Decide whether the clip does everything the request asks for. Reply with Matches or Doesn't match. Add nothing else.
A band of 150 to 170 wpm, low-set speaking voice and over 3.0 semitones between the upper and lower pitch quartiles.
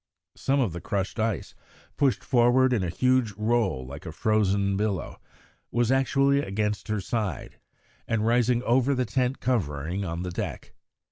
Matches